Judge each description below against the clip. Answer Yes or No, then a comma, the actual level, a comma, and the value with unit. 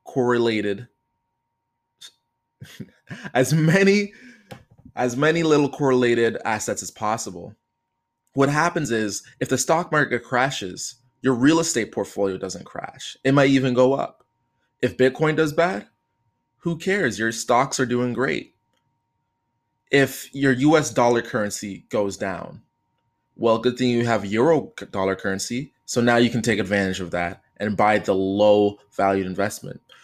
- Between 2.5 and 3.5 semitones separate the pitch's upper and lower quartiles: No, average, 4.5 semitones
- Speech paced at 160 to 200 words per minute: No, average, 140 wpm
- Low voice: Yes, low, 120 Hz